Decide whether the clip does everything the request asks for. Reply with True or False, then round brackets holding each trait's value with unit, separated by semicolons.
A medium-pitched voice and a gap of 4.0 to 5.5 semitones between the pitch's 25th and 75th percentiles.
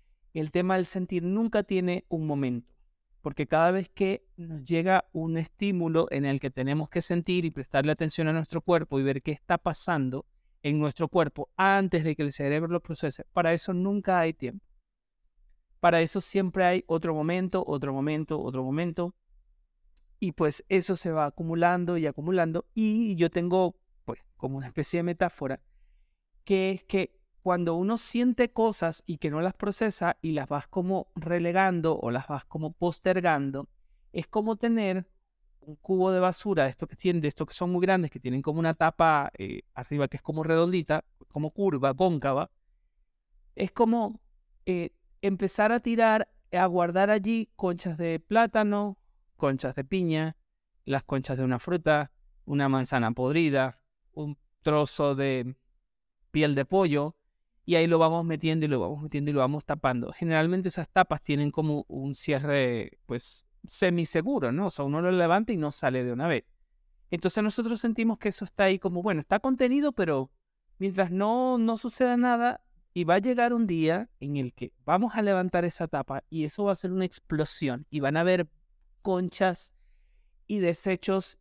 True (165 Hz; 4.5 semitones)